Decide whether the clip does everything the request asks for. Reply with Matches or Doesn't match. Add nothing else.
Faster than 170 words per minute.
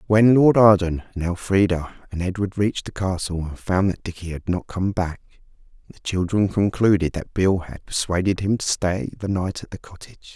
Matches